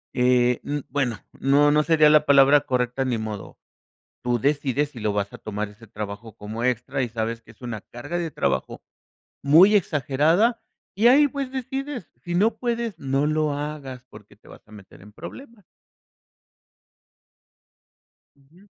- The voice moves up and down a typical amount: No, wide, 5.9 semitones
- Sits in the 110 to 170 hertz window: Yes, medium, 140 Hz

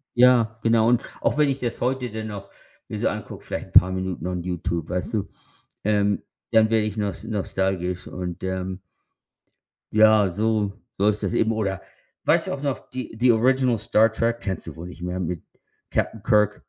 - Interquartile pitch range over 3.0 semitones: Yes, average, 3.6 semitones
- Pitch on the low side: Yes, low, 105 Hz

